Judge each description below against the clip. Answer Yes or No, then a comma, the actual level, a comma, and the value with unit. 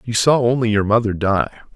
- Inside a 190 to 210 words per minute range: Yes, fast, 205 wpm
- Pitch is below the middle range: Yes, low, 110 Hz